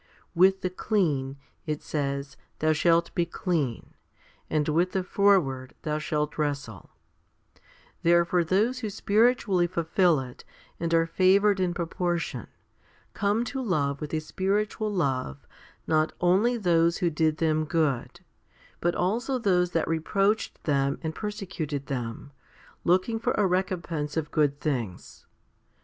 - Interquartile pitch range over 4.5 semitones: No, average, 4.2 semitones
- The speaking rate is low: Yes, slow, 130 wpm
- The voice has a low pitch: No, medium, 170 Hz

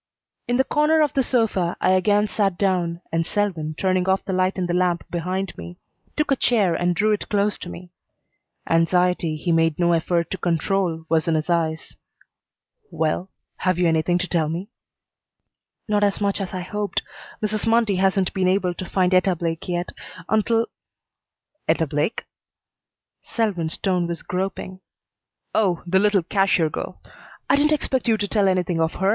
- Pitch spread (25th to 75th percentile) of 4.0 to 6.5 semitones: No, average, 3.1 semitones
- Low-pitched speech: No, medium, 185 Hz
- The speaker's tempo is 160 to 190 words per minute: Yes, average, 175 wpm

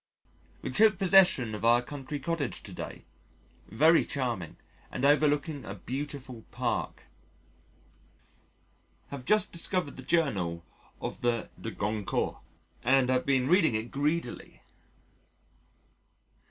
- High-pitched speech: No, low, 135 Hz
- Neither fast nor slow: No, slow, 110 wpm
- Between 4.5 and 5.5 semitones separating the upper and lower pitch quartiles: Yes, average, 5.0 semitones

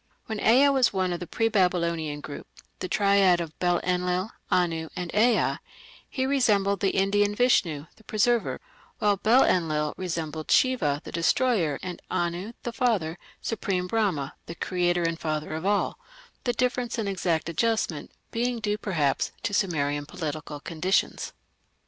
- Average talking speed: Yes, average, 150 wpm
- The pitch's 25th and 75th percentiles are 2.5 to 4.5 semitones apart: No, average, 4.9 semitones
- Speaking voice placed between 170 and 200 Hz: Yes, medium, 185 Hz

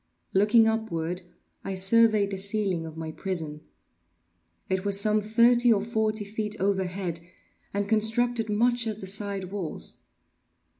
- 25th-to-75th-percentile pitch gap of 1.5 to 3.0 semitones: Yes, narrow, 2.6 semitones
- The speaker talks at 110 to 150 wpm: Yes, slow, 135 wpm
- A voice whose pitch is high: Yes, high, 205 Hz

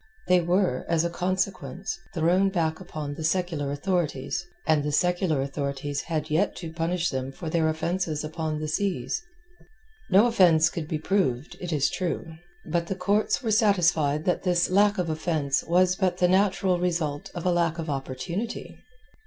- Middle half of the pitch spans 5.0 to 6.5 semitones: No, average, 3.1 semitones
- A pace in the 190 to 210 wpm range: No, average, 170 wpm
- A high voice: No, medium, 170 Hz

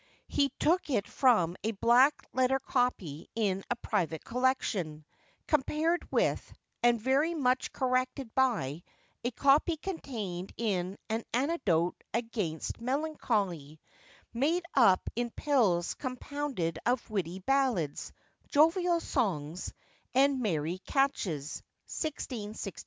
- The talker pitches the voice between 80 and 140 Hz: No, high, 240 Hz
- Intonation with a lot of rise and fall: Yes, wide, 6.8 semitones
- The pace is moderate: No, slow, 110 wpm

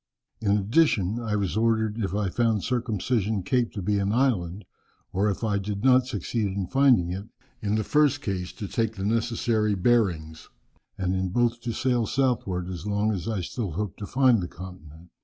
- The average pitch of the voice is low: Yes, low, 105 Hz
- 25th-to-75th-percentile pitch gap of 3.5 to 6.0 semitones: Yes, average, 3.8 semitones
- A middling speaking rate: Yes, average, 190 wpm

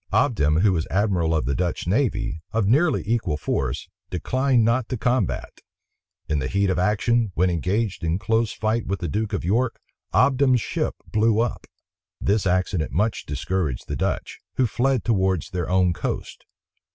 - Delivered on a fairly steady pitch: No, average, 4.6 semitones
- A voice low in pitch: Yes, low, 100 Hz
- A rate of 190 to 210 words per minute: No, average, 165 wpm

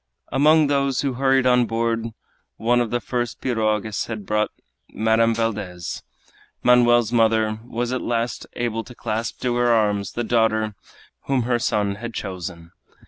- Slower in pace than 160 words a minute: Yes, average, 150 wpm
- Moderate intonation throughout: No, narrow, 2.1 semitones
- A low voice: Yes, low, 115 Hz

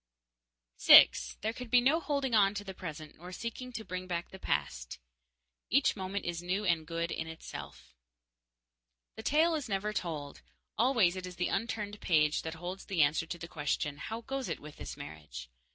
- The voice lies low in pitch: No, medium, 185 Hz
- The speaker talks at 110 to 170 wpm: No, average, 185 wpm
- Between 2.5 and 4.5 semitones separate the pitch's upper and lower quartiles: No, wide, 5.4 semitones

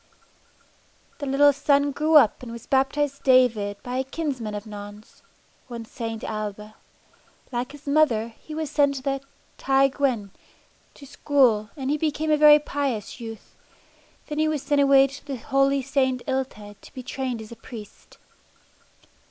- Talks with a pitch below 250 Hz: No, very high, 265 Hz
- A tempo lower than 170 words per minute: Yes, average, 160 wpm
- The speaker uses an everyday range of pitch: Yes, average, 3.9 semitones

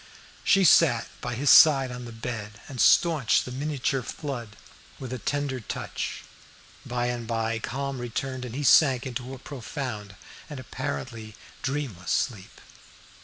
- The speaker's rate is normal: Yes, average, 145 wpm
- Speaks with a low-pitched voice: Yes, low, 125 Hz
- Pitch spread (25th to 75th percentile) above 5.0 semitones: No, average, 3.1 semitones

